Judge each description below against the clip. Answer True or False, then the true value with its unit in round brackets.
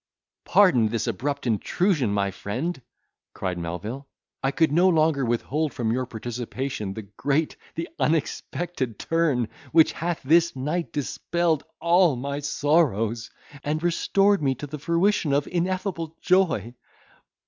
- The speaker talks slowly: True (130 wpm)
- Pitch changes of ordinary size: False (5.7 semitones)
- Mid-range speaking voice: True (145 Hz)